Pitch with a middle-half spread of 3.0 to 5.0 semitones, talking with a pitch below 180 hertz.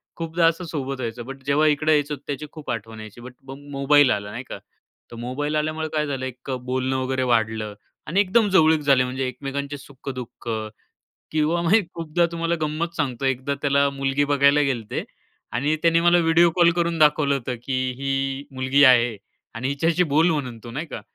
Yes: average, 3.3 semitones; medium, 140 Hz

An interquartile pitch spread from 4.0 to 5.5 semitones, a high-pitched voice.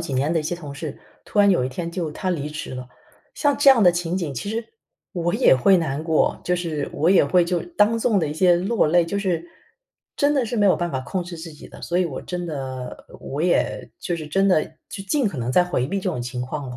No: average, 4.3 semitones; medium, 170 Hz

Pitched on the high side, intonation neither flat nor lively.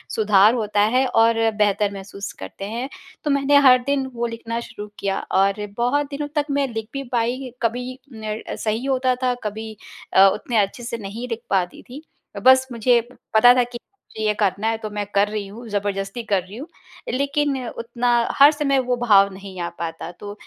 Yes: high, 230 Hz; average, 3.8 semitones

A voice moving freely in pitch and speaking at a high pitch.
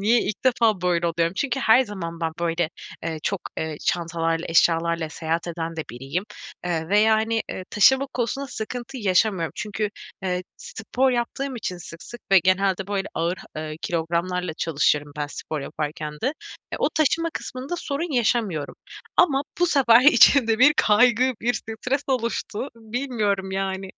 Yes: wide, 6.4 semitones; high, 200 Hz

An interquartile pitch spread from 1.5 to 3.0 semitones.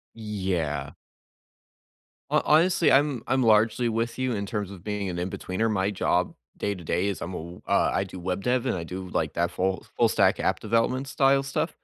No: average, 4.5 semitones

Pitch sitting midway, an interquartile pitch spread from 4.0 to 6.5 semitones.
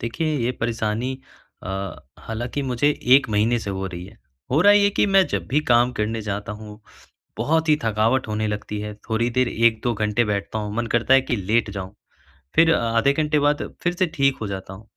No: low, 115 Hz; average, 4.6 semitones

